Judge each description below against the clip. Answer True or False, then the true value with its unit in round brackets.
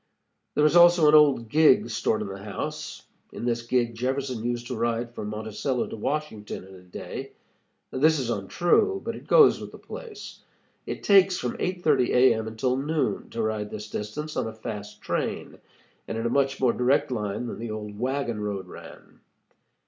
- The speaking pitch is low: True (120 Hz)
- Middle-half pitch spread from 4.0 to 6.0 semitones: True (4.9 semitones)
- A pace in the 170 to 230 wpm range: True (185 wpm)